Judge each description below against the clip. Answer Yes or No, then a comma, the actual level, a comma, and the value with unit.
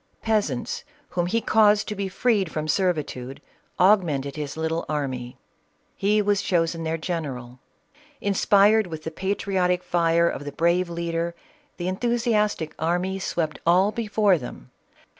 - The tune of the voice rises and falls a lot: No, average, 4.0 semitones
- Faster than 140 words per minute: No, slow, 135 wpm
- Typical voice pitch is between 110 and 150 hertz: No, medium, 175 Hz